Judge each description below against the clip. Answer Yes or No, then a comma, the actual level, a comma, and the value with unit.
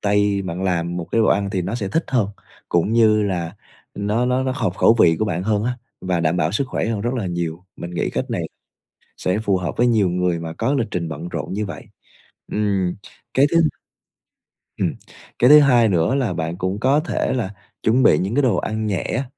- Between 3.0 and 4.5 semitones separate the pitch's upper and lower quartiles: No, average, 4.9 semitones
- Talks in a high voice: No, low, 100 Hz